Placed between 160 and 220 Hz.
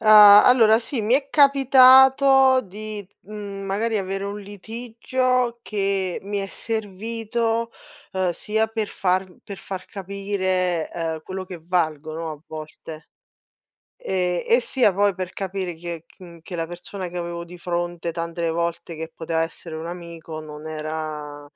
Yes: high, 190 Hz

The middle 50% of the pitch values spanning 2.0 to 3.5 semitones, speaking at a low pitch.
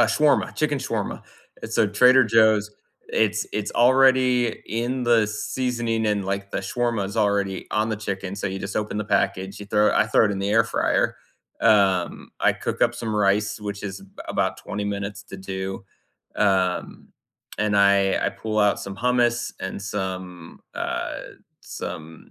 Yes: narrow, 2.5 semitones; low, 105 Hz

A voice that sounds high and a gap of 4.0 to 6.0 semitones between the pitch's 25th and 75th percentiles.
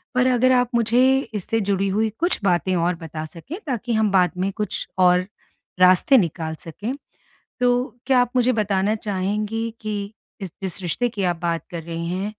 Yes: high, 205 Hz; average, 4.8 semitones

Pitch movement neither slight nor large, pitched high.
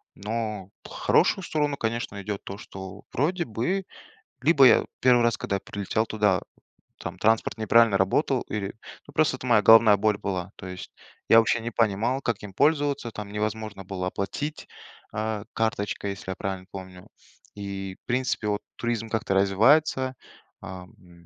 No: average, 3.4 semitones; low, 110 Hz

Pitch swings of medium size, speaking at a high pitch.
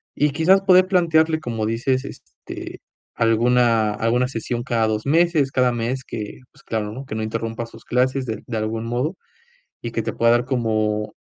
No: average, 3.3 semitones; low, 120 Hz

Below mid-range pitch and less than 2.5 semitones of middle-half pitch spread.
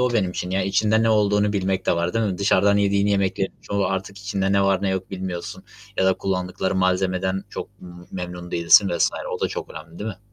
Yes: very low, 95 Hz; narrow, 1.5 semitones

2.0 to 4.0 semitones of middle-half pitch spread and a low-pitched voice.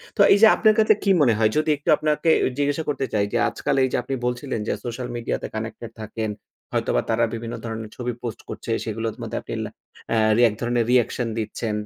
Yes: average, 3.4 semitones; low, 120 Hz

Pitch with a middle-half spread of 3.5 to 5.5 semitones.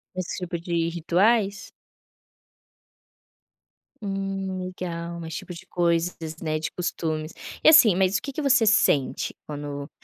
No: average, 2.9 semitones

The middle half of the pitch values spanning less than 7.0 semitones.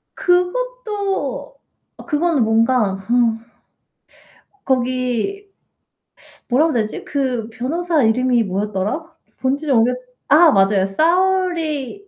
No: wide, 7.4 semitones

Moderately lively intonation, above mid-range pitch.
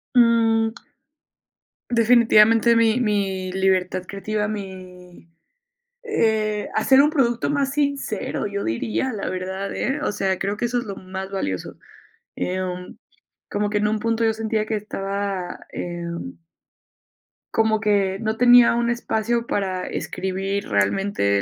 Yes: average, 3.2 semitones; high, 210 Hz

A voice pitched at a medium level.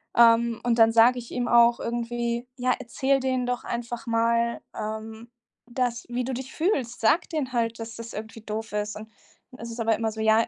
No: high, 235 Hz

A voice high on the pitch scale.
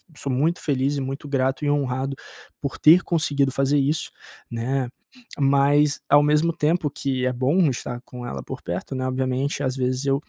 No: low, 135 Hz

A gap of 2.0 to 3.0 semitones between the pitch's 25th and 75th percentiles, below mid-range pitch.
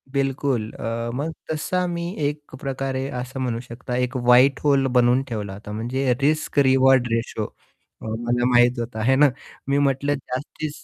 Yes: narrow, 2.6 semitones; low, 130 Hz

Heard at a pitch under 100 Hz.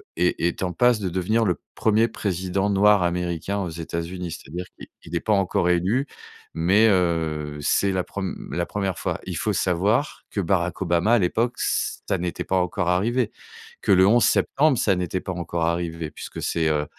Yes: very low, 90 Hz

